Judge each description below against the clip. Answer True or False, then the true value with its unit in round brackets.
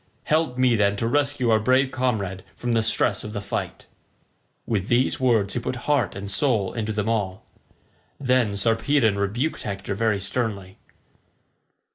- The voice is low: True (110 Hz)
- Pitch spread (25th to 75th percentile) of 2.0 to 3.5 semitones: False (4.0 semitones)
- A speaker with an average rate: True (155 wpm)